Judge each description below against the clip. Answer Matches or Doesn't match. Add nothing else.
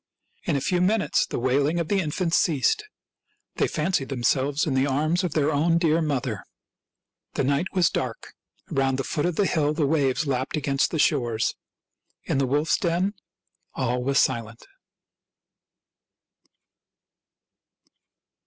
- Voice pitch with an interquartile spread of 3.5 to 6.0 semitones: Matches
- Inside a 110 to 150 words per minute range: Matches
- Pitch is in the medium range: Matches